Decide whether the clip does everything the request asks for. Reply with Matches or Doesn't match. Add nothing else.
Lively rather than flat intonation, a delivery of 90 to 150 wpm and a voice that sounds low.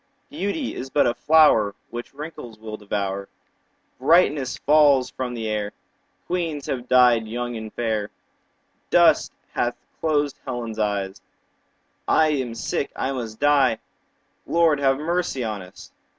Doesn't match